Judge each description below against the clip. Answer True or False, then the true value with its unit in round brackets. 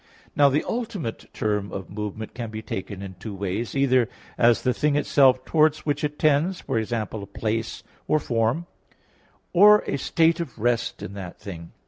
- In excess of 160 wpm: True (170 wpm)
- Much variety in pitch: True (5.8 semitones)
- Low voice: True (120 Hz)